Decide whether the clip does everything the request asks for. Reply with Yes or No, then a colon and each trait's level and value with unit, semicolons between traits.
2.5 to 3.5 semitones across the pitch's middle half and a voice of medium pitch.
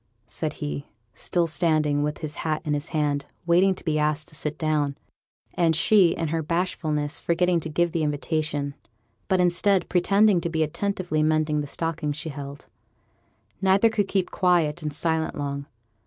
Yes: average, 2.8 semitones; medium, 160 Hz